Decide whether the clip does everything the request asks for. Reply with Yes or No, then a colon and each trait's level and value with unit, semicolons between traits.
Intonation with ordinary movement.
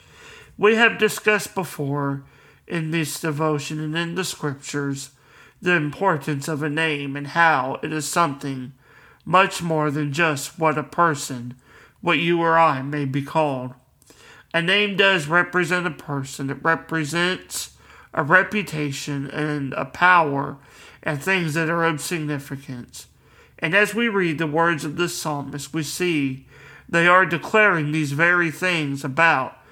Yes: average, 3.3 semitones